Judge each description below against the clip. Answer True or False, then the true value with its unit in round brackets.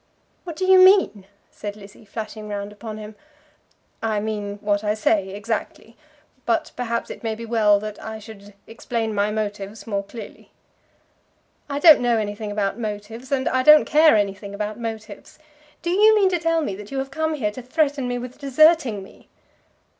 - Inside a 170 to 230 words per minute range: True (180 wpm)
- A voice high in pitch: True (220 Hz)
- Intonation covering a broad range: False (4.4 semitones)